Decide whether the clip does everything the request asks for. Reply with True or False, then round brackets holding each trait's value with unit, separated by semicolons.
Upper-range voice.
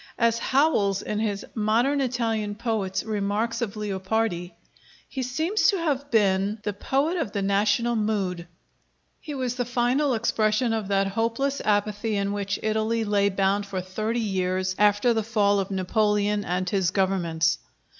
True (210 Hz)